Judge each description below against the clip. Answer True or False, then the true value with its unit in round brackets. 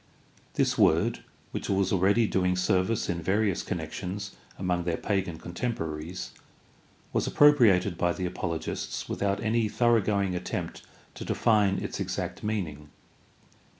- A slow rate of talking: True (125 wpm)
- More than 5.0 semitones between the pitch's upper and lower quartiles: False (3.1 semitones)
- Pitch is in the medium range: False (95 Hz)